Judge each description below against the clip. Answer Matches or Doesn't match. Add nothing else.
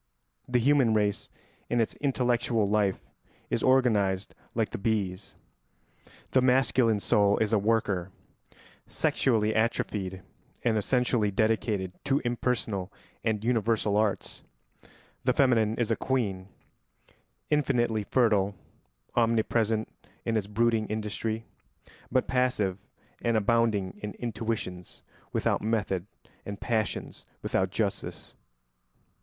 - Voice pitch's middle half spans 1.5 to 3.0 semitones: Matches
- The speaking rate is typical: Doesn't match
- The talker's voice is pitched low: Matches